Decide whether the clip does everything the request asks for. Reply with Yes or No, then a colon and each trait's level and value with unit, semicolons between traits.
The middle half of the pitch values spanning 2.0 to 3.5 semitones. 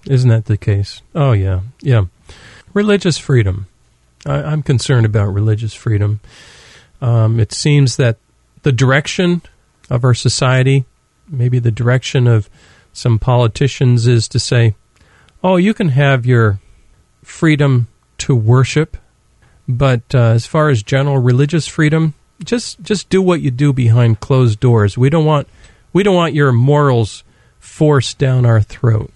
No: average, 4.2 semitones